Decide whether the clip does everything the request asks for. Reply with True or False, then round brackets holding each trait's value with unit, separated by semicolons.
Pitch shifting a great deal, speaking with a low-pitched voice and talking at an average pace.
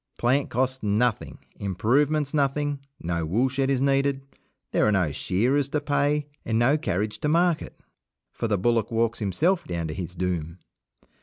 True (6.2 semitones; 125 Hz; 155 wpm)